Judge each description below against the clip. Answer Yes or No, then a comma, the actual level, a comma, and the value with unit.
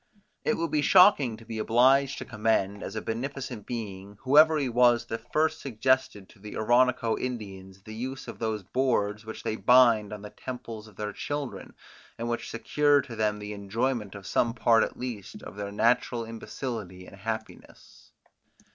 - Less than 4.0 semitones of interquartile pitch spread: Yes, average, 3.5 semitones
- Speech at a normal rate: Yes, average, 175 wpm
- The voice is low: Yes, low, 115 Hz